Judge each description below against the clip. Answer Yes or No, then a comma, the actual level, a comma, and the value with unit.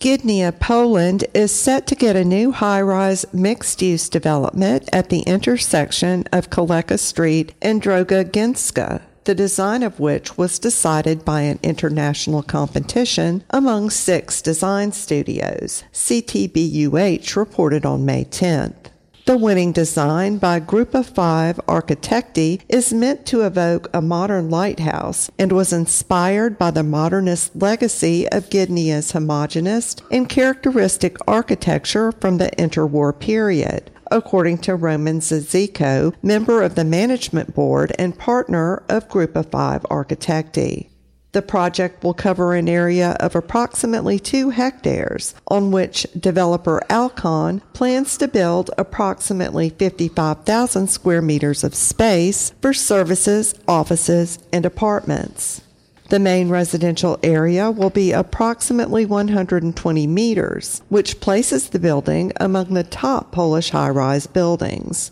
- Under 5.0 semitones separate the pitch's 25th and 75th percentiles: Yes, average, 4.0 semitones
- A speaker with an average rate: No, slow, 125 wpm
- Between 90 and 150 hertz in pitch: No, medium, 180 Hz